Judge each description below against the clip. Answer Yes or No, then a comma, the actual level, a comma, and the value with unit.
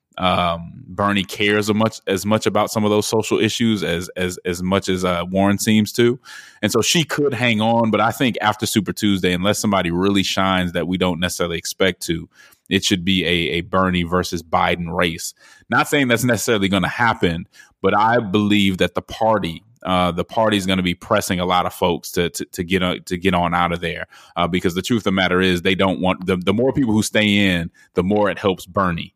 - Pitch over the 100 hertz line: No, very low, 95 Hz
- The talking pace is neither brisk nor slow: No, fast, 230 wpm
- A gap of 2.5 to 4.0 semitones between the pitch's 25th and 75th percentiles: Yes, average, 2.8 semitones